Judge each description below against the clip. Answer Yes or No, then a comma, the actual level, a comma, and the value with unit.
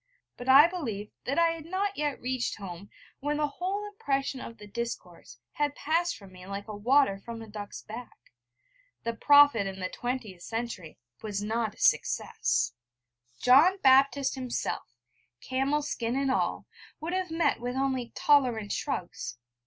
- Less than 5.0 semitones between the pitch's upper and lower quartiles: No, wide, 5.4 semitones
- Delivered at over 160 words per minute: No, average, 155 wpm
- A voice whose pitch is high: Yes, very high, 255 Hz